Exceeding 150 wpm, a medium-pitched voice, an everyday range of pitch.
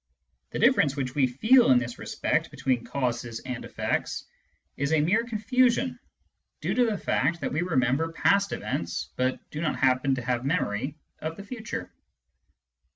No: average, 160 wpm; medium, 145 Hz; wide, 7.8 semitones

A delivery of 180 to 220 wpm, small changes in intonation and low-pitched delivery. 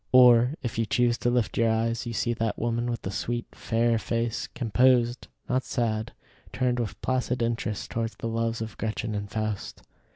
Yes: average, 185 wpm; narrow, 1.4 semitones; low, 115 Hz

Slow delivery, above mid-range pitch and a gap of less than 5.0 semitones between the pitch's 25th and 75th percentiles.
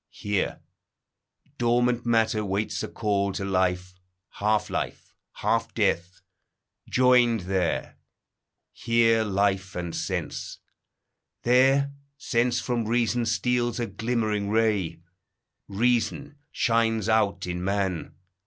No: slow, 100 wpm; low, 110 Hz; average, 3.4 semitones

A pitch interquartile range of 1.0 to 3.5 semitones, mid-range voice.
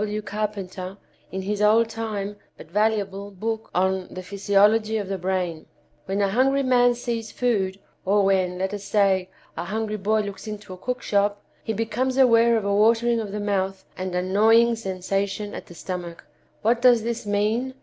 No: average, 2.8 semitones; high, 205 Hz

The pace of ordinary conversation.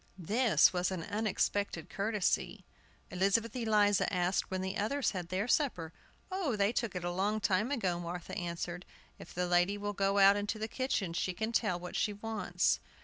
Yes: average, 180 wpm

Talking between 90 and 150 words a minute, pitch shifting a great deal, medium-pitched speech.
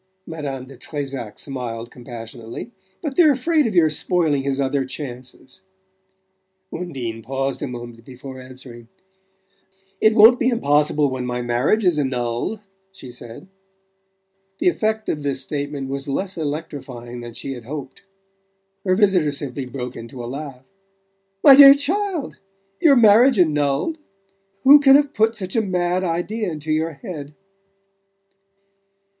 Yes: average, 140 wpm; wide, 7.4 semitones; medium, 145 Hz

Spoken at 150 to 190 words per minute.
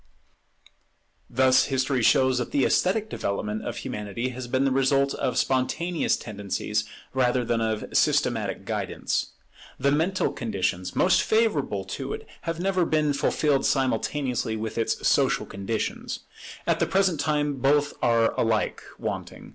No: average, 140 wpm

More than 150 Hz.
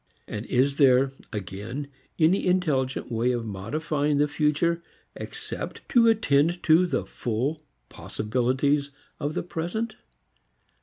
No: medium, 145 Hz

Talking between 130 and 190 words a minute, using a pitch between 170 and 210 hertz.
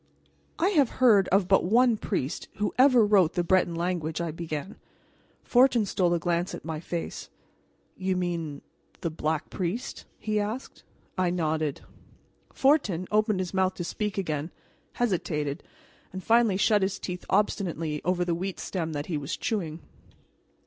Yes: average, 155 wpm; medium, 185 Hz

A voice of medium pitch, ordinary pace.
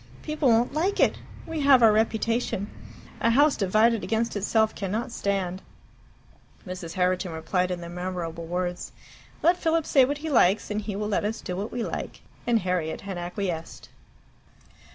No: high, 210 Hz; average, 165 wpm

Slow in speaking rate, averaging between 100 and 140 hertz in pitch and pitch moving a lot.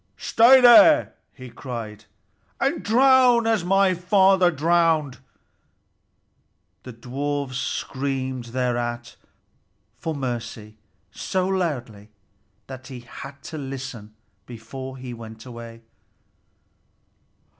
Yes: slow, 90 wpm; low, 135 Hz; wide, 6.8 semitones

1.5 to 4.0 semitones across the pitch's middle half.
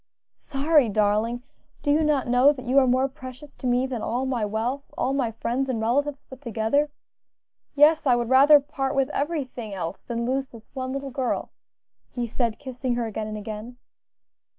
Yes: average, 2.9 semitones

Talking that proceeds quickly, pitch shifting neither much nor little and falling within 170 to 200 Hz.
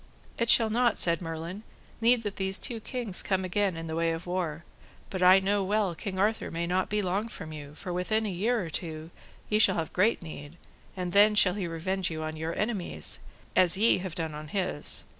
Yes: fast, 215 wpm; average, 3.9 semitones; medium, 185 Hz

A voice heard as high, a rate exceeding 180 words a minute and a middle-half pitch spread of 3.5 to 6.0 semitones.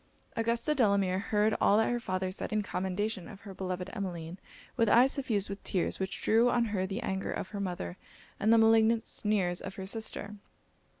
No: high, 200 Hz; average, 190 wpm; average, 2.9 semitones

